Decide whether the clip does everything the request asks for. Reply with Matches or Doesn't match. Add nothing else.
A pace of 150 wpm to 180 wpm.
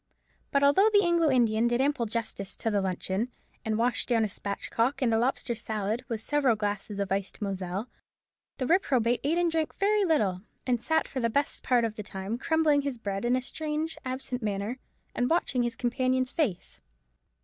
Doesn't match